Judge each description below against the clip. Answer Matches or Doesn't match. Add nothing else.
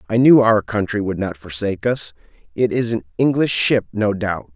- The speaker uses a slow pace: Doesn't match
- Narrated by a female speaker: Doesn't match